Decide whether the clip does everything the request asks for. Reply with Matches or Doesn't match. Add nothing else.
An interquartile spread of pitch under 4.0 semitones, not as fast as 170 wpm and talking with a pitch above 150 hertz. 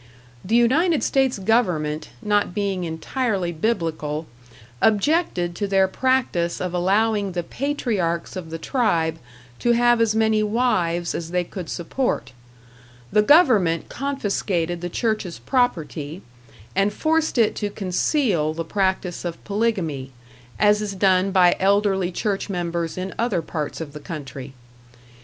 Doesn't match